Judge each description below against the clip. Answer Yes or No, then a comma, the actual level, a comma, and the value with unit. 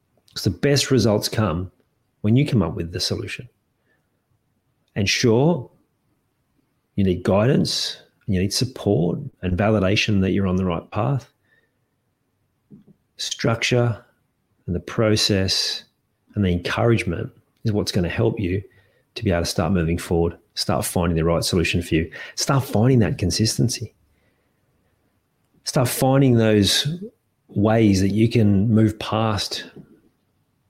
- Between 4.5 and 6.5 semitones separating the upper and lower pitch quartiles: No, average, 4.1 semitones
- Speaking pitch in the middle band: No, low, 110 Hz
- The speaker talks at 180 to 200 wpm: No, slow, 135 wpm